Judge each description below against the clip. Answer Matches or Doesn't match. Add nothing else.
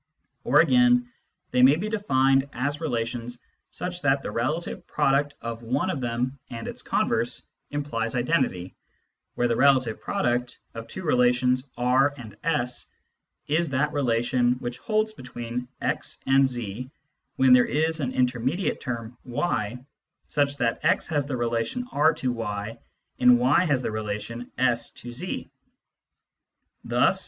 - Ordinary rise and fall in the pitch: Matches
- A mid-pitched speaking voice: Doesn't match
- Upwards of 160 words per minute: Doesn't match